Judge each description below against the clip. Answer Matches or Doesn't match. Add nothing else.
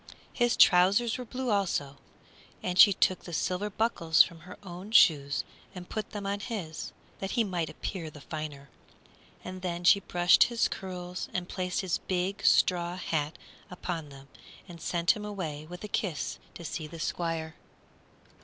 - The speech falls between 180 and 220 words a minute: Doesn't match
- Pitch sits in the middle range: Matches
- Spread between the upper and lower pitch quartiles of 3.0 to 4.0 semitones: Matches